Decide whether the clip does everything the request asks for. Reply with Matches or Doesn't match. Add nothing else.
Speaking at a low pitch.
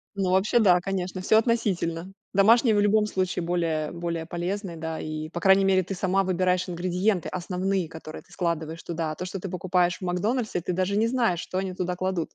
Doesn't match